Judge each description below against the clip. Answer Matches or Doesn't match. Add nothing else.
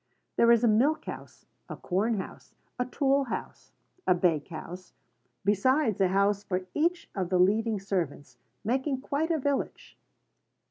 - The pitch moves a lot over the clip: Matches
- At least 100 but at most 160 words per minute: Matches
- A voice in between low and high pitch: Doesn't match